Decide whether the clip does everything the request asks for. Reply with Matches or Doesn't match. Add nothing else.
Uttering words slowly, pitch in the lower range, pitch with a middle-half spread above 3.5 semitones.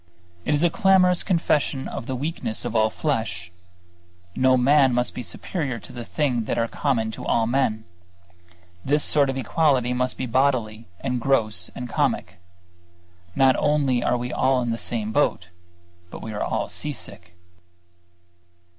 Doesn't match